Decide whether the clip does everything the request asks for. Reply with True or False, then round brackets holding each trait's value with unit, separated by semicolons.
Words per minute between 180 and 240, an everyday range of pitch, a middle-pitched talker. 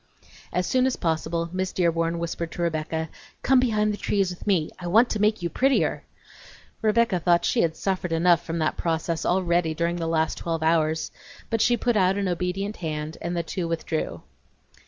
True (190 wpm; 3.1 semitones; 175 Hz)